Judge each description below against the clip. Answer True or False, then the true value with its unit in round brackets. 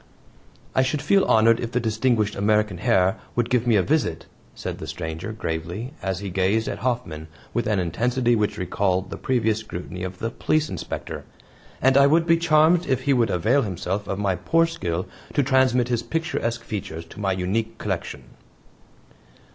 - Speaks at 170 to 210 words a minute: True (180 wpm)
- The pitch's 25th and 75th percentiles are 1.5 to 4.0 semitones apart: False (5.5 semitones)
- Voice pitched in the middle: False (110 Hz)